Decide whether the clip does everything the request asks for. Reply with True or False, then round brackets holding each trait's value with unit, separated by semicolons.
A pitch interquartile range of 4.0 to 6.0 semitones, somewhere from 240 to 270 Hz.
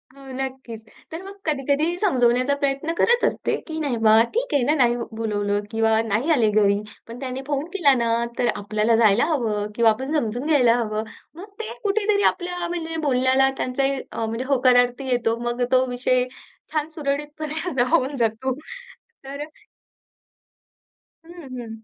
True (4.8 semitones; 260 Hz)